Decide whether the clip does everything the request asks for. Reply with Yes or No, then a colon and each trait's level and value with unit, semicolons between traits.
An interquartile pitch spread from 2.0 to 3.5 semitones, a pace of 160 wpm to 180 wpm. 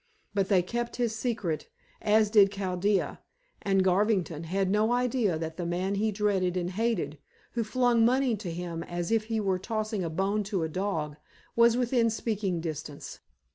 No: average, 4.0 semitones; average, 175 wpm